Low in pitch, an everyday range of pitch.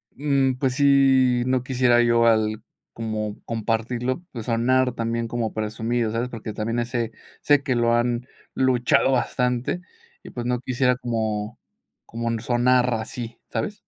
No: low, 120 Hz; narrow, 1.8 semitones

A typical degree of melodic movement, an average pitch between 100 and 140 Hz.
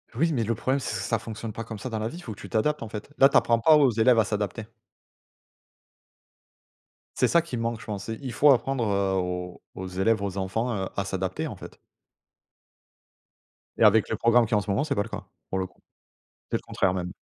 Yes: average, 3.4 semitones; low, 110 Hz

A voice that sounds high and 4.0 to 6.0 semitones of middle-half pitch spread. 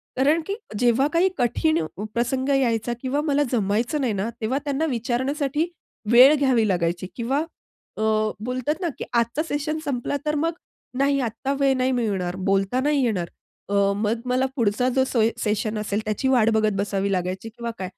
Yes: high, 245 Hz; average, 4.4 semitones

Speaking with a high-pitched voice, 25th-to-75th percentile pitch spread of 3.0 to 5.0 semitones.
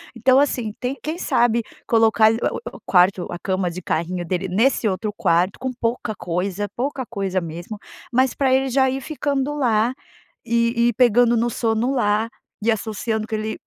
Yes: high, 225 Hz; average, 4.2 semitones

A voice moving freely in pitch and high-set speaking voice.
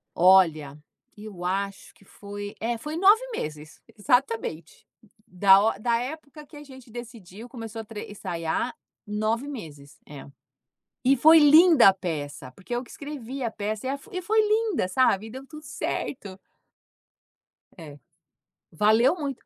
Yes: wide, 6.4 semitones; high, 225 Hz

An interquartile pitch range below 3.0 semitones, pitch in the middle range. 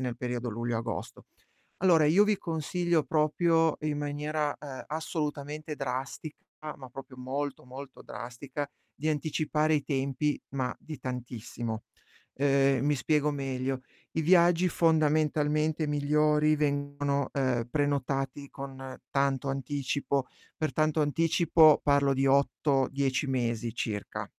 Yes: narrow, 2.6 semitones; medium, 145 Hz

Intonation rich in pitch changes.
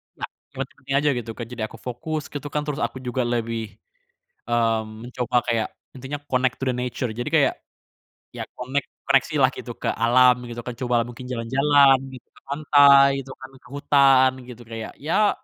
No: average, 2.7 semitones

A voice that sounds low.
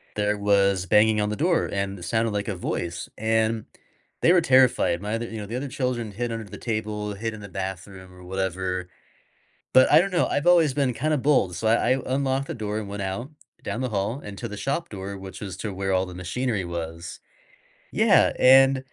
Yes: low, 105 Hz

